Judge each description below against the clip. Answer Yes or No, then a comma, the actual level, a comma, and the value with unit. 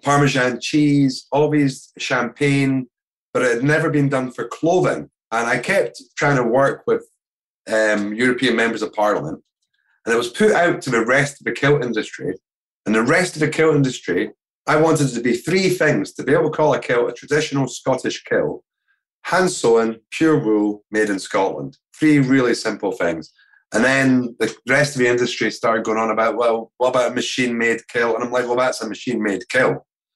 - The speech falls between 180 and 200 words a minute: Yes, average, 195 wpm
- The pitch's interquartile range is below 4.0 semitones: No, average, 4.7 semitones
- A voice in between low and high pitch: No, low, 130 Hz